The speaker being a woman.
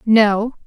Yes: female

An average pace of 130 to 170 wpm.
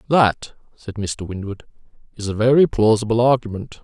Yes: average, 140 wpm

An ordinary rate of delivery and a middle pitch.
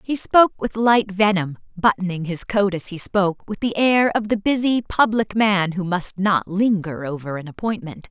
No: average, 190 wpm; high, 200 Hz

